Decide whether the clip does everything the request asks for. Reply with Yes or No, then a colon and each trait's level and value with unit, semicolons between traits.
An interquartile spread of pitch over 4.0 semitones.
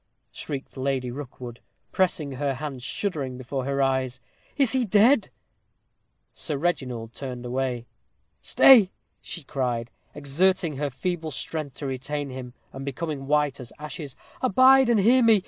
Yes: average, 5.2 semitones